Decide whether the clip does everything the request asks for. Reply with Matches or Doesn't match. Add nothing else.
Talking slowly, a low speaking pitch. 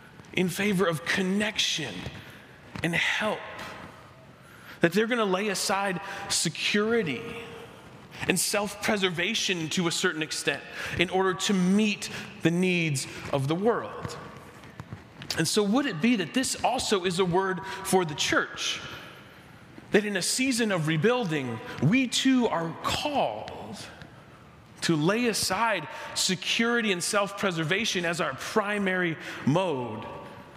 Doesn't match